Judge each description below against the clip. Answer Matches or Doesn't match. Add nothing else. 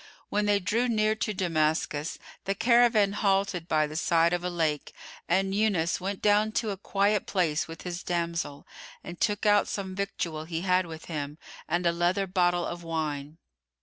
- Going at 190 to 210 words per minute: Doesn't match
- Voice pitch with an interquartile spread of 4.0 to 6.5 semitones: Doesn't match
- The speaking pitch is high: Doesn't match